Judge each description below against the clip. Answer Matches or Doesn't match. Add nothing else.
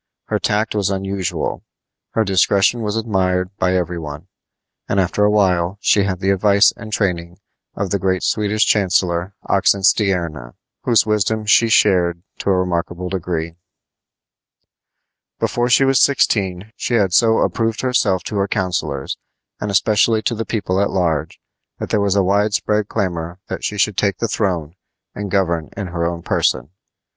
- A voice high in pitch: Doesn't match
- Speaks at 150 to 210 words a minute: Matches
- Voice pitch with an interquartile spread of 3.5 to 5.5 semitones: Doesn't match